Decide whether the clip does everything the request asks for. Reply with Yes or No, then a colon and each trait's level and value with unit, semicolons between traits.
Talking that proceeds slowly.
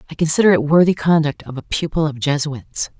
No: average, 200 wpm